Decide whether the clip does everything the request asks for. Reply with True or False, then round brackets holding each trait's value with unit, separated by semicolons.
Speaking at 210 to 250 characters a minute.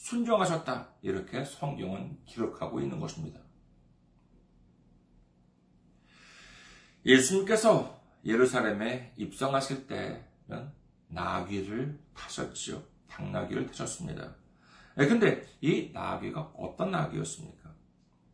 True (215 characters per minute)